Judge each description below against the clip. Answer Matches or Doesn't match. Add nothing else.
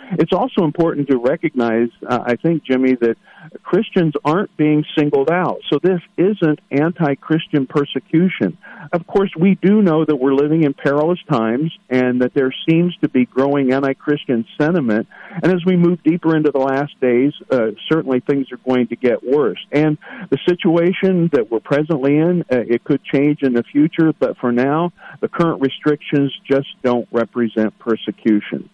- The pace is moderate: Matches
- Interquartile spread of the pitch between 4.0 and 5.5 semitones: Matches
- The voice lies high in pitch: Doesn't match